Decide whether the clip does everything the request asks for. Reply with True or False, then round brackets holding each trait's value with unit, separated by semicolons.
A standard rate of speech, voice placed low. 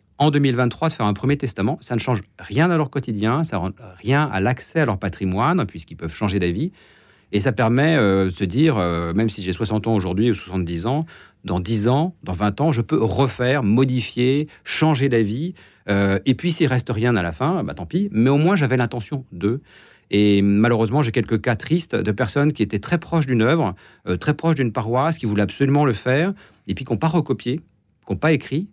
False (225 wpm; 120 Hz)